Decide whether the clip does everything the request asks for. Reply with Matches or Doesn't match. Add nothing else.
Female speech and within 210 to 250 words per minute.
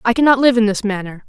Doesn't match